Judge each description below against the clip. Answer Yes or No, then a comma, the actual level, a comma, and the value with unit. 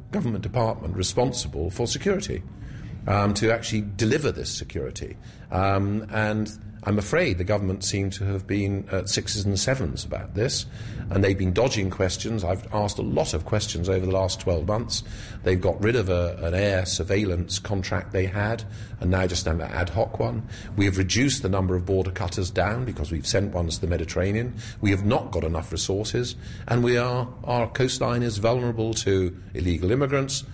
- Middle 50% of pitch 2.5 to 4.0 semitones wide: Yes, average, 3.1 semitones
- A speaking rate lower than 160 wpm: No, average, 185 wpm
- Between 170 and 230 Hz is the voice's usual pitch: No, low, 100 Hz